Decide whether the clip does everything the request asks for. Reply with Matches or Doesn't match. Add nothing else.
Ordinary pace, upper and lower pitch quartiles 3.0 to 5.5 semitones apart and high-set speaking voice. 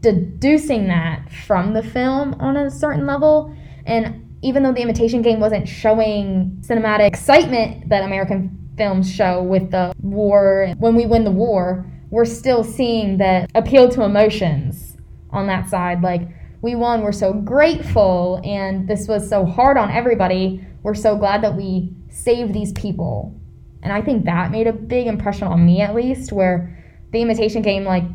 Matches